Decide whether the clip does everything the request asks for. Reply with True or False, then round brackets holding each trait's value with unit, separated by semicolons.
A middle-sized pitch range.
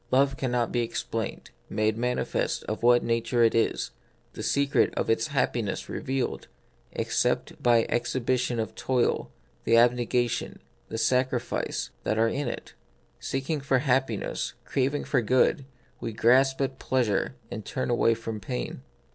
False (2.3 semitones)